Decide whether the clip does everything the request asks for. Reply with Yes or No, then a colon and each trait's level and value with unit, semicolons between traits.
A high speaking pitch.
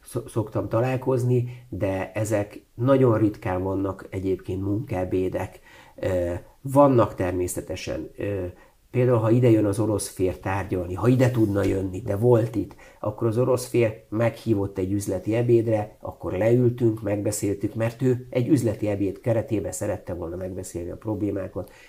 No: low, 105 Hz